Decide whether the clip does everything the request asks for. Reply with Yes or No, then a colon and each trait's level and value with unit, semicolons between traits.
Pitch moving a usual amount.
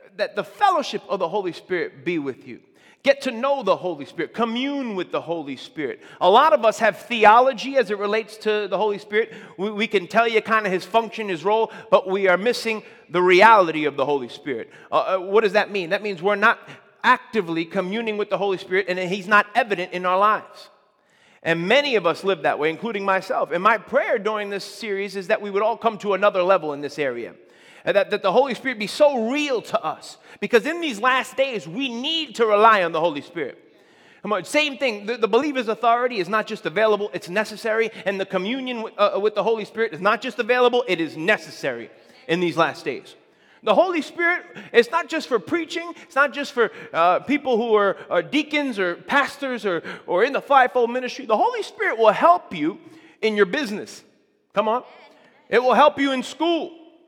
Yes: average, 5.0 semitones